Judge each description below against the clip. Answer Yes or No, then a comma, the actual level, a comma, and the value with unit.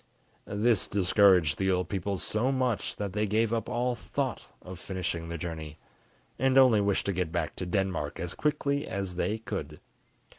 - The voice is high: No, low, 100 Hz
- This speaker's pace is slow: No, average, 175 wpm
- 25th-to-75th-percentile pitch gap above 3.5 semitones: Yes, average, 4.1 semitones